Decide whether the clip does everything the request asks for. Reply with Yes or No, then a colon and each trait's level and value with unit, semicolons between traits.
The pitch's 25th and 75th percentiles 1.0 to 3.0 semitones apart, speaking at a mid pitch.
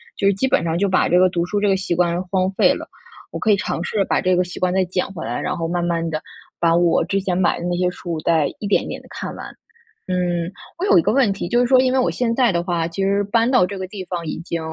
Yes: average, 2.7 semitones; medium, 180 Hz